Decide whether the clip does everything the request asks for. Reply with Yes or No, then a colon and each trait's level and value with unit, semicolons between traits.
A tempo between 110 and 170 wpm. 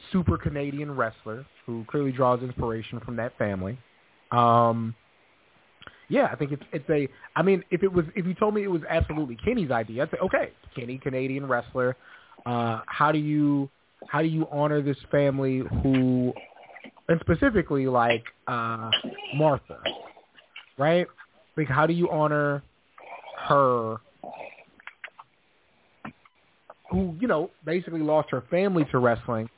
Yes: average, 140 wpm